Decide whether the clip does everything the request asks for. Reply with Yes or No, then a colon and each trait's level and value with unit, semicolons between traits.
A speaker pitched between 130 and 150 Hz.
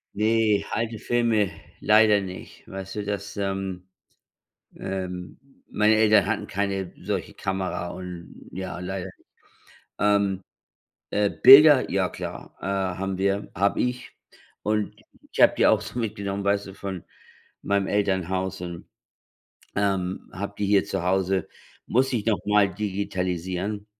No: low, 100 Hz